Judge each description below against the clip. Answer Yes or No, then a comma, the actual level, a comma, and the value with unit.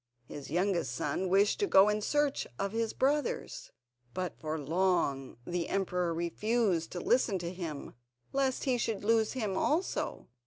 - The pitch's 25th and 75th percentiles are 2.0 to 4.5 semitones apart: No, average, 5.1 semitones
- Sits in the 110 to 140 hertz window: No, high, 190 Hz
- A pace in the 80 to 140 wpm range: No, average, 155 wpm